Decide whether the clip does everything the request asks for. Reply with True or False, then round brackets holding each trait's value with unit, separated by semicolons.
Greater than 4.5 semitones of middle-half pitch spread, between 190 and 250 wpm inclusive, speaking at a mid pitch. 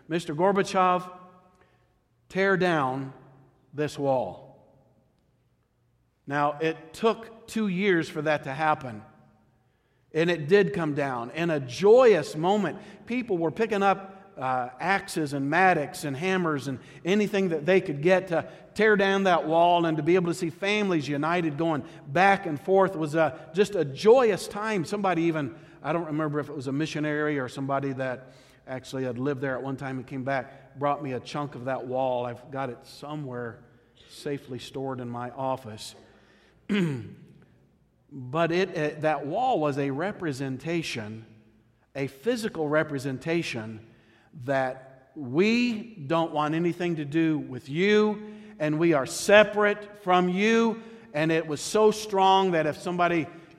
False (5.6 semitones; 150 wpm; 155 Hz)